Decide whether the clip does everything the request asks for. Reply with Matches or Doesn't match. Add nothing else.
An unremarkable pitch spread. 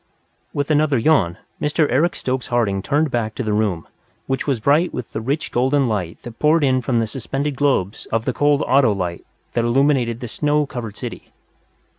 Matches